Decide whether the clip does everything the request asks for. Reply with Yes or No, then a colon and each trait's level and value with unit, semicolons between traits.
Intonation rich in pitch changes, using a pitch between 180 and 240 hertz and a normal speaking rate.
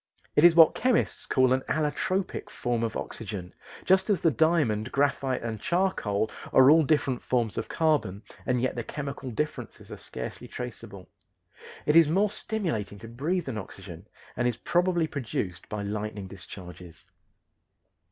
No: wide, 7.0 semitones; low, 130 Hz; average, 150 wpm